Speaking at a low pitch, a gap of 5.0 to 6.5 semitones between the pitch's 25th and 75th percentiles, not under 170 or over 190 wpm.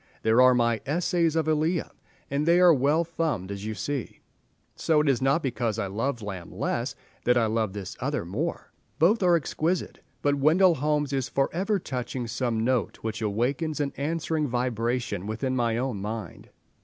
Yes: low, 130 Hz; wide, 5.6 semitones; average, 180 wpm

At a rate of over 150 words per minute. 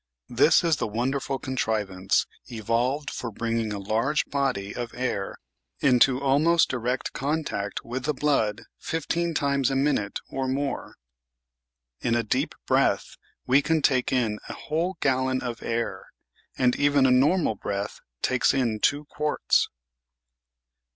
No: slow, 135 wpm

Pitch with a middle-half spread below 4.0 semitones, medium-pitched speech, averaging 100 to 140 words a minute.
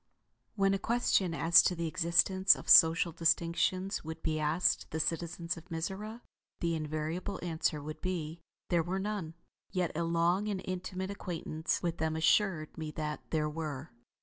No: average, 2.7 semitones; medium, 170 Hz; average, 160 wpm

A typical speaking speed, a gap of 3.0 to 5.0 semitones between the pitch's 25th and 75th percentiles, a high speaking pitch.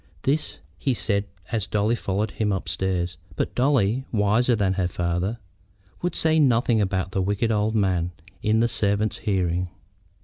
No: average, 150 wpm; average, 3.4 semitones; low, 105 Hz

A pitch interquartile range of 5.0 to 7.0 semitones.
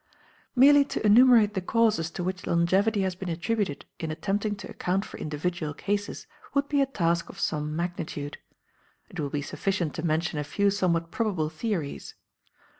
No: average, 4.3 semitones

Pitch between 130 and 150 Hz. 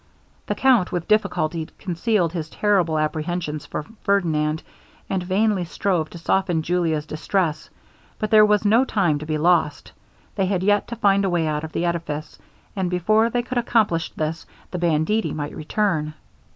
No: medium, 175 Hz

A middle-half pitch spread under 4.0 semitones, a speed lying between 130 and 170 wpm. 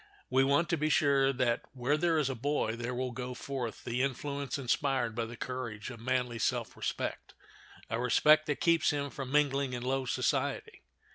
No: average, 2.7 semitones; average, 185 wpm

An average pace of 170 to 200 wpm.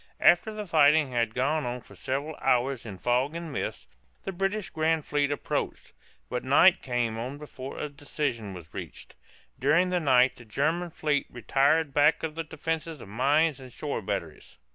Yes: average, 175 wpm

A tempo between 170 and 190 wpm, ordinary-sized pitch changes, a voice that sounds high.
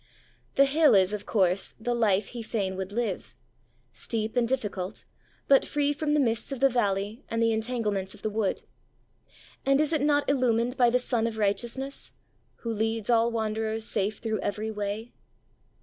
Yes: average, 175 wpm; average, 3.1 semitones; high, 225 Hz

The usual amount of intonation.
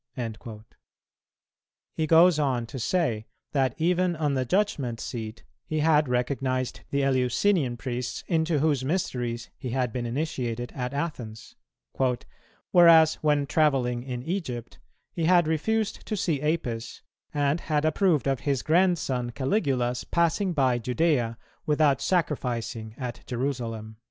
Yes: average, 4.7 semitones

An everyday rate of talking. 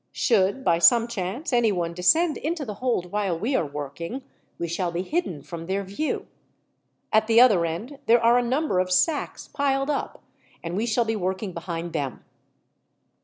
Yes: average, 175 wpm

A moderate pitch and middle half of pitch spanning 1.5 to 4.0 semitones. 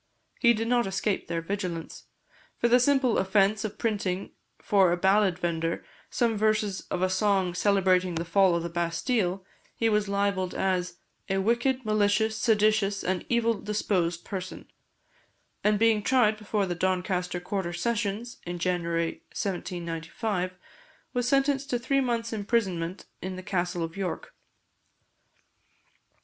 No: high, 195 Hz; average, 3.4 semitones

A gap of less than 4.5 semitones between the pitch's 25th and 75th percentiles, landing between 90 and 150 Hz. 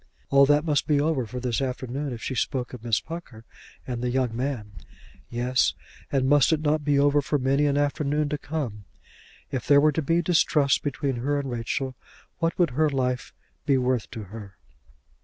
Yes: average, 2.9 semitones; low, 135 Hz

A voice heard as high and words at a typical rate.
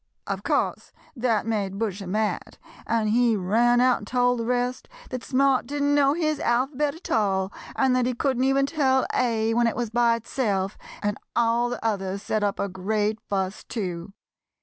Yes: high, 230 Hz; average, 185 wpm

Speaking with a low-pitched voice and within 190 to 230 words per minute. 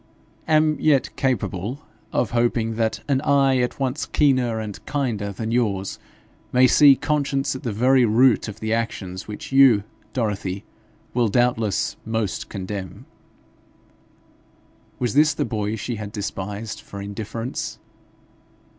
No: low, 115 Hz; slow, 135 wpm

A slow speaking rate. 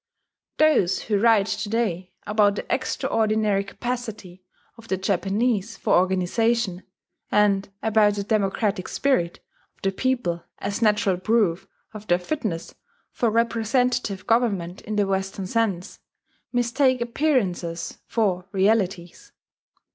Yes: slow, 115 wpm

